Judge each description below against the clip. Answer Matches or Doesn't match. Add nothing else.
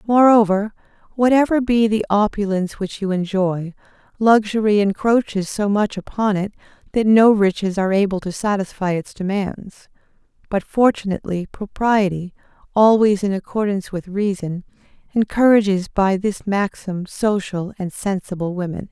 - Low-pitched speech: Doesn't match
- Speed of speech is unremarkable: Doesn't match